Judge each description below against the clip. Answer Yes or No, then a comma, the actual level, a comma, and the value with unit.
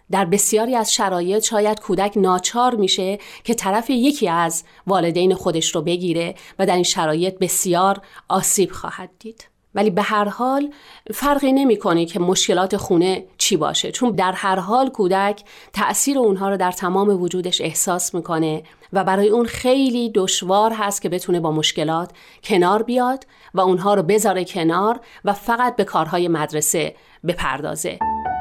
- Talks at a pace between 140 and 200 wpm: Yes, average, 150 wpm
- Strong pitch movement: No, average, 3.3 semitones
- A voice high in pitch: Yes, high, 195 Hz